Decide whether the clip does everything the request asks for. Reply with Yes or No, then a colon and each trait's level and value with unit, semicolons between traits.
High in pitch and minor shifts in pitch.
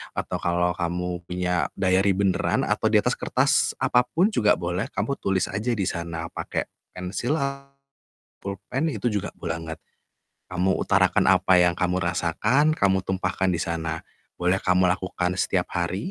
No: very low, 90 Hz; narrow, 2.2 semitones